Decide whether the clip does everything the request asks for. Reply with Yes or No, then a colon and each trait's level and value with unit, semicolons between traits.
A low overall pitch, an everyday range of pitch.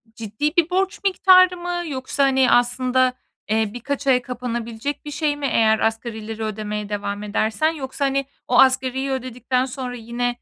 No: very high, 255 Hz; average, 4.0 semitones